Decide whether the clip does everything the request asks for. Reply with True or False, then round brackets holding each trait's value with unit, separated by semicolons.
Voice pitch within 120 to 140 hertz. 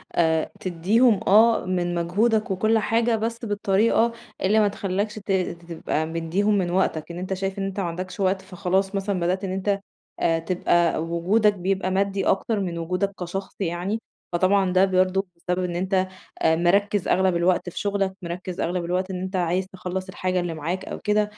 False (190 Hz)